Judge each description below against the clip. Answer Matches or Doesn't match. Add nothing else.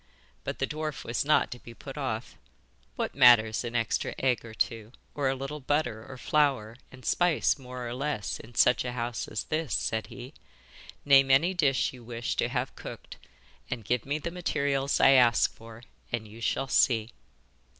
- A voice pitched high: Doesn't match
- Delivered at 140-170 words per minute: Doesn't match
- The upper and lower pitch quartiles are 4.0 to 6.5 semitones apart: Doesn't match